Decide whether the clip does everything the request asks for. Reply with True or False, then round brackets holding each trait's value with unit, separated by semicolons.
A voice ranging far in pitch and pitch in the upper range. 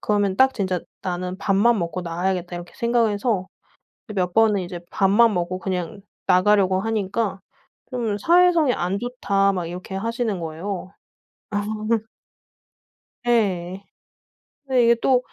False (3.8 semitones; 195 Hz)